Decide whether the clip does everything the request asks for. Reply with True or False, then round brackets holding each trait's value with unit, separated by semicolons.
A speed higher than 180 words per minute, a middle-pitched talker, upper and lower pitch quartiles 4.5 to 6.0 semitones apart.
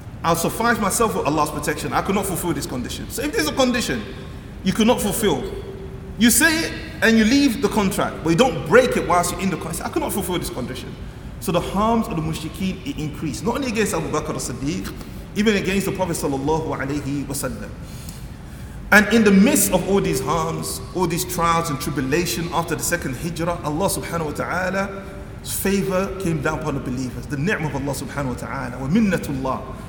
True (195 wpm; 170 Hz; 5.5 semitones)